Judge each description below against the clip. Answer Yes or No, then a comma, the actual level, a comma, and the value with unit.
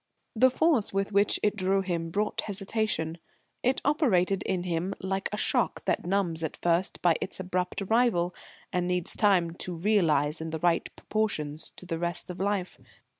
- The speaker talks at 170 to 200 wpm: Yes, average, 175 wpm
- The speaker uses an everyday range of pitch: Yes, average, 3.2 semitones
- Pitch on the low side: No, medium, 185 Hz